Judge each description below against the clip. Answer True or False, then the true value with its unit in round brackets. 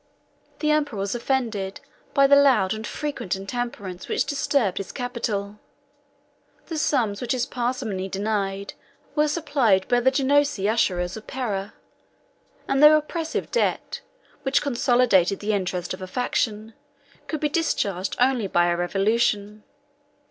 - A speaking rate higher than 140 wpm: False (135 wpm)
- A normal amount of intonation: False (5.7 semitones)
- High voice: True (230 Hz)